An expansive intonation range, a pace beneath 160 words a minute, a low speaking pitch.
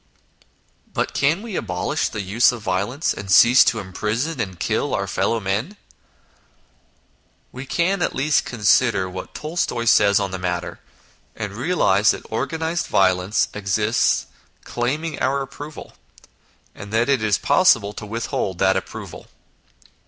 Yes: wide, 6.2 semitones; average, 145 wpm; low, 115 Hz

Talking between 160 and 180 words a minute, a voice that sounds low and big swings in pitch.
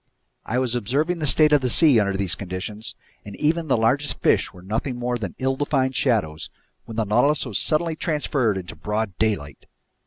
No: average, 190 wpm; low, 120 Hz; wide, 6.0 semitones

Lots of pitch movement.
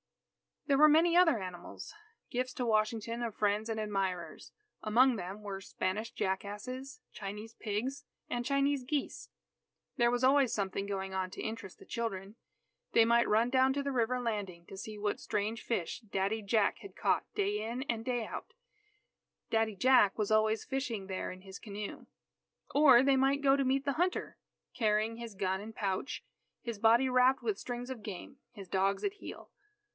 No: average, 4.3 semitones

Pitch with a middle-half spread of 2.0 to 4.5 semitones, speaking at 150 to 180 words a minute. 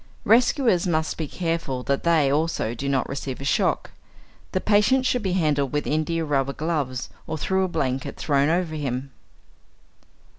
Yes: average, 4.2 semitones; average, 160 wpm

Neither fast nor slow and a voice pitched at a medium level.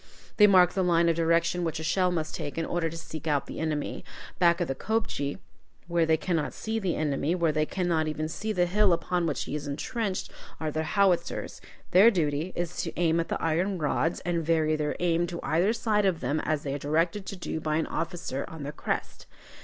No: fast, 225 wpm; medium, 165 Hz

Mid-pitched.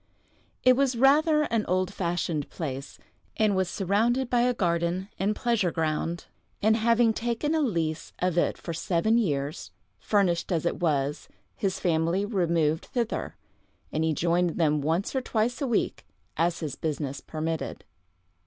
Yes: medium, 180 Hz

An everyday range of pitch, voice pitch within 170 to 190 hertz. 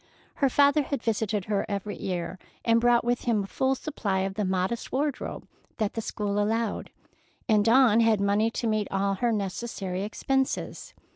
No: average, 3.1 semitones; high, 215 Hz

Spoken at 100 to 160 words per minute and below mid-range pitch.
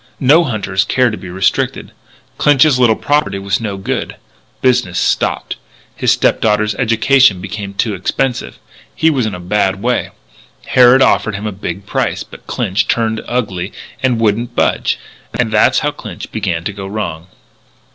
Yes: average, 155 wpm; low, 110 Hz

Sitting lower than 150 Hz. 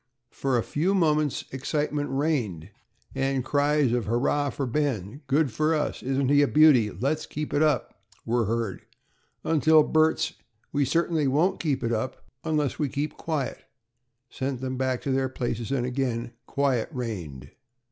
Yes: low, 135 Hz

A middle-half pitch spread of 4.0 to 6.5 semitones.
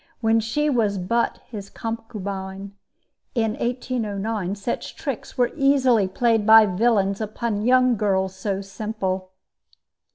No: average, 3.2 semitones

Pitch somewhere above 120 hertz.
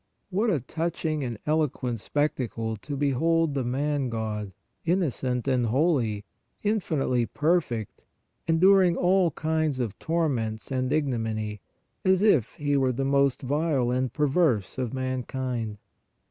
Yes: low, 135 Hz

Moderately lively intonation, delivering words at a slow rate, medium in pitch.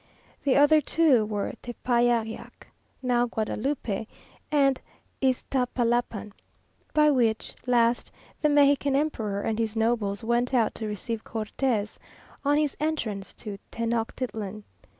No: average, 3.8 semitones; slow, 110 wpm; high, 240 Hz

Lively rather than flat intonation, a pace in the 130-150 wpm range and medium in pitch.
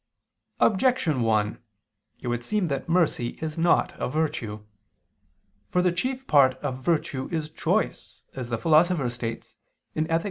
Yes: wide, 5.9 semitones; average, 140 wpm; medium, 150 Hz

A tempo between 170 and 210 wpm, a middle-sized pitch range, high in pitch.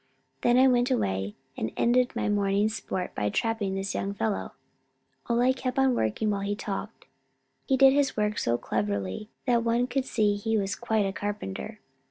Yes: average, 180 wpm; average, 3.9 semitones; high, 210 Hz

